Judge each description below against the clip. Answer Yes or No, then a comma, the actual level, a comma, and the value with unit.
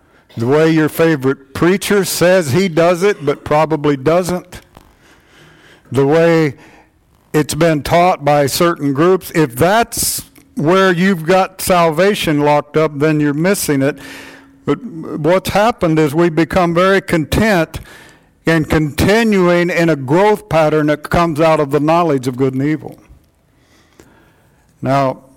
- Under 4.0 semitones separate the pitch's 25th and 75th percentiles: Yes, average, 3.3 semitones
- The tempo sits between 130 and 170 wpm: Yes, slow, 135 wpm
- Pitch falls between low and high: Yes, medium, 160 Hz